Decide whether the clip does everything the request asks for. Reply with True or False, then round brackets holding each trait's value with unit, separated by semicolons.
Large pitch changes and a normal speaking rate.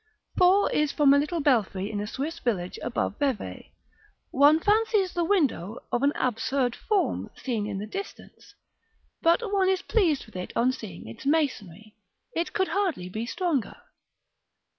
True (8.3 semitones; 160 wpm)